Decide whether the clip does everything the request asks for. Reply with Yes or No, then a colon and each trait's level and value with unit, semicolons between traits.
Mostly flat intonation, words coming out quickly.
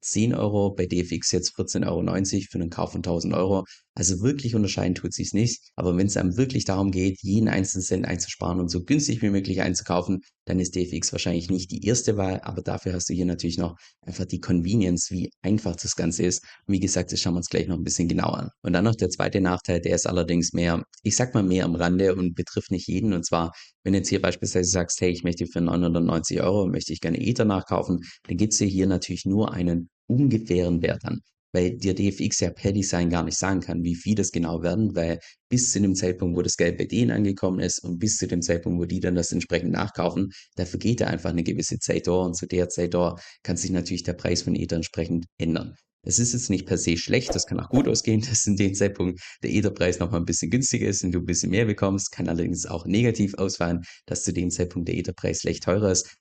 Yes: narrow, 2.3 semitones; fast, 240 wpm